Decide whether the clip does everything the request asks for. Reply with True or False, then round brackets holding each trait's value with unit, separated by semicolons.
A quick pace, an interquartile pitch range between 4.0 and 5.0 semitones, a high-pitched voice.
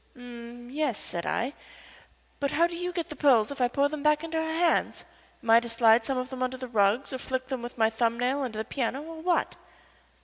True (240 wpm; 4.3 semitones; 255 Hz)